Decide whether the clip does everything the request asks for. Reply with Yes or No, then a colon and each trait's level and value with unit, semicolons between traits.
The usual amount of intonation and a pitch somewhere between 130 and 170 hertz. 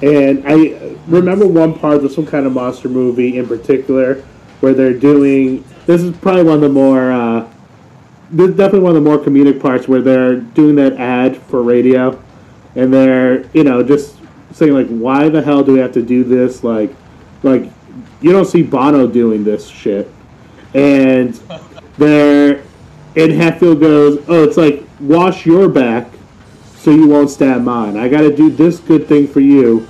Yes: average, 3.3 semitones; medium, 140 Hz